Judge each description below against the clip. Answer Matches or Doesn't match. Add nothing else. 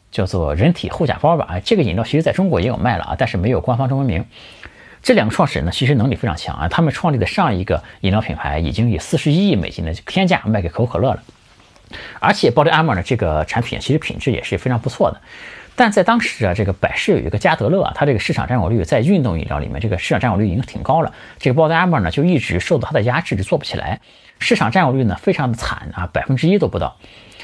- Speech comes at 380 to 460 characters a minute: Matches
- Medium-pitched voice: Doesn't match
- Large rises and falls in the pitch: Matches